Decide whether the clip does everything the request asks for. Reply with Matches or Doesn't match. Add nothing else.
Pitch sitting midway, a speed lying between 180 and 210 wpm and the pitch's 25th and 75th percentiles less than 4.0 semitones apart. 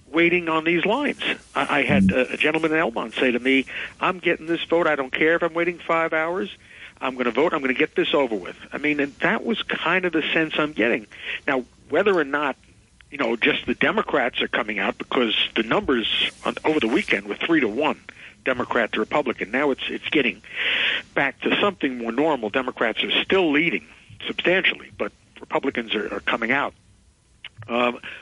Matches